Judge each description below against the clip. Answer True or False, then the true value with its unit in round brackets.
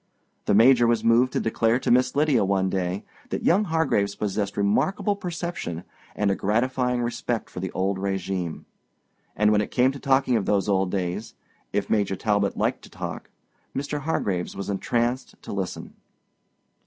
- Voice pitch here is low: True (105 Hz)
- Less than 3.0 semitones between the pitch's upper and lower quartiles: False (4.8 semitones)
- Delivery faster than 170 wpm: False (165 wpm)